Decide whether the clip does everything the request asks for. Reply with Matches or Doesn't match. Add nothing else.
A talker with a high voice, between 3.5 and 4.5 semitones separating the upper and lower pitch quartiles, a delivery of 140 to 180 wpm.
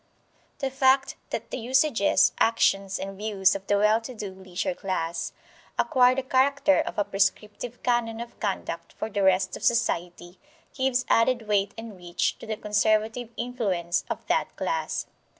Matches